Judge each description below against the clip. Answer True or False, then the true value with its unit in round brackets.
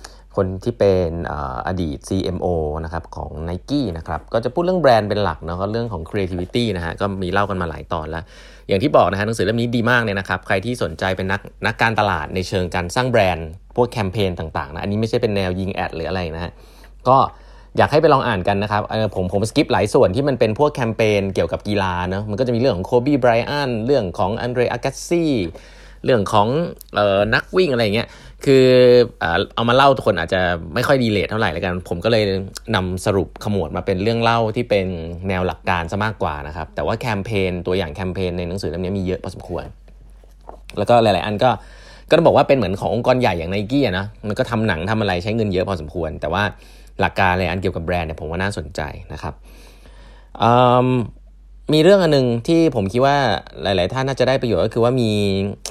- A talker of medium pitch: False (100 Hz)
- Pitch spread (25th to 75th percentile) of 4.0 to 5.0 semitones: True (4.5 semitones)